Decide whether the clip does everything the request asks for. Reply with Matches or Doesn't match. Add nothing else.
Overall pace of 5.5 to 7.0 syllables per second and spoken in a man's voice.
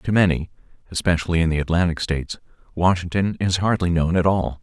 Matches